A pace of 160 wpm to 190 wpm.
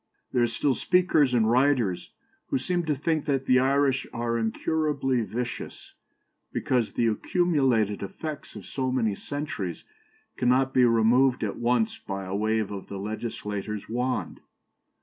No: average, 145 wpm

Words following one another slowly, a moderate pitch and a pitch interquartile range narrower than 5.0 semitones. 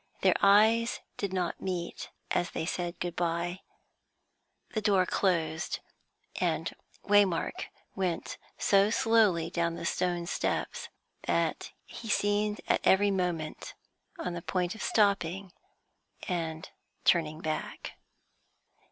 Yes: slow, 115 wpm; medium, 180 Hz; average, 3.2 semitones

